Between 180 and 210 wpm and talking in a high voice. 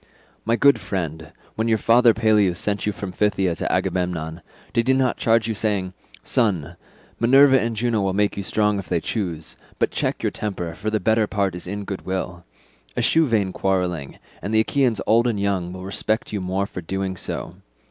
No: average, 195 wpm; low, 100 Hz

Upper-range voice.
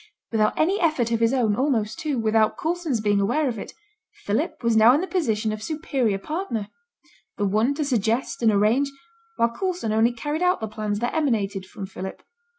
Yes: high, 230 Hz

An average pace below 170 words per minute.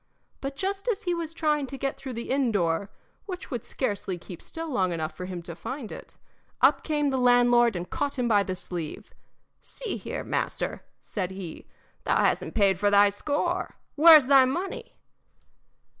No: average, 180 wpm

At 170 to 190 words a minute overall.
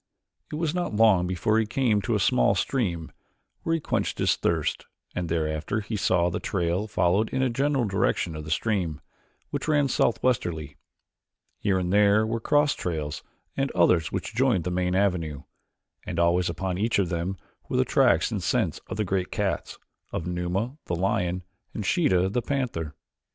Yes: average, 180 wpm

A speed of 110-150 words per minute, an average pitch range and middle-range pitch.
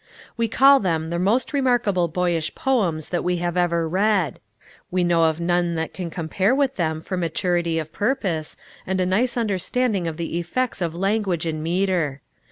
No: average, 175 wpm; average, 3.6 semitones; medium, 180 Hz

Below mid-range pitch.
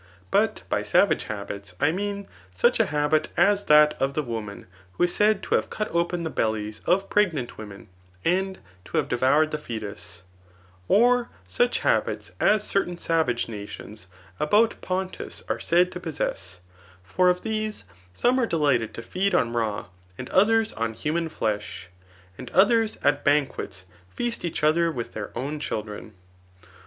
No: medium, 155 Hz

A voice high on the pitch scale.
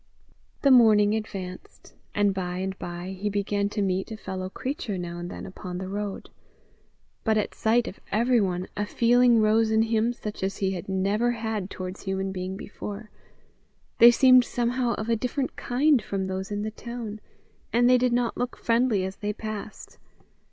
Yes: high, 210 Hz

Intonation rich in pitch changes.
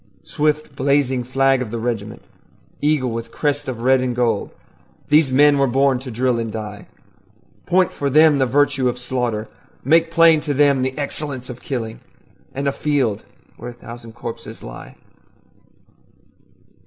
No: average, 3.3 semitones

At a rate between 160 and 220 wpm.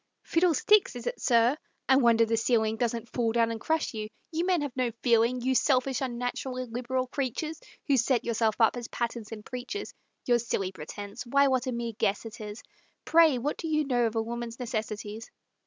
Yes: average, 195 wpm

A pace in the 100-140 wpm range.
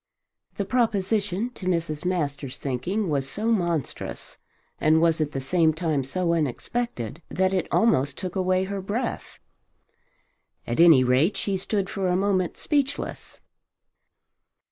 Yes: slow, 135 wpm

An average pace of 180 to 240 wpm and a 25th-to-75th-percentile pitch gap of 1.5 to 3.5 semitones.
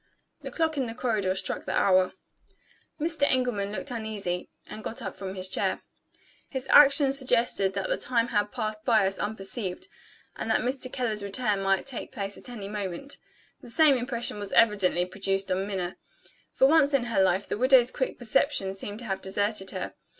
No: average, 185 wpm; average, 4.6 semitones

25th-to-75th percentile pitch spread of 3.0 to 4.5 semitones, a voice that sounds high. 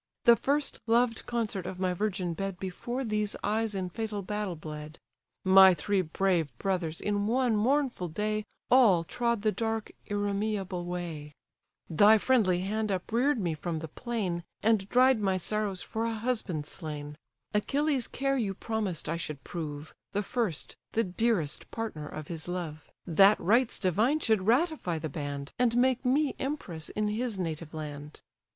No: average, 5.0 semitones; high, 200 Hz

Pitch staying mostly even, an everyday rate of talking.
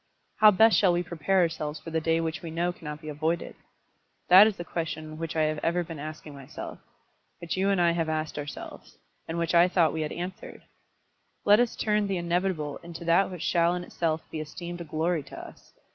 No: narrow, 2.2 semitones; fast, 215 wpm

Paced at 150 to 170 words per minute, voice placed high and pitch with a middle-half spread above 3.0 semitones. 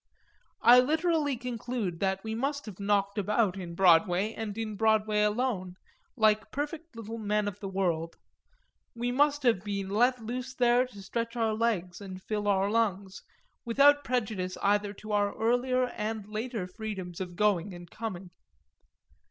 Yes: average, 155 wpm; high, 215 Hz; average, 3.7 semitones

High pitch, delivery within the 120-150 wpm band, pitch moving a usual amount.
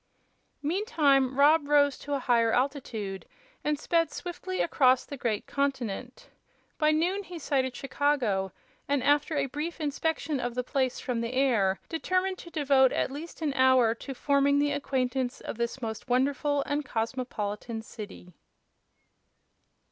Yes: very high, 275 Hz; average, 145 wpm; average, 3.2 semitones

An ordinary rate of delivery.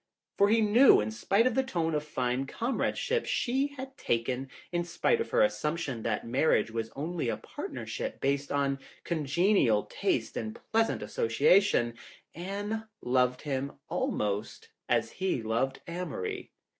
Yes: average, 150 wpm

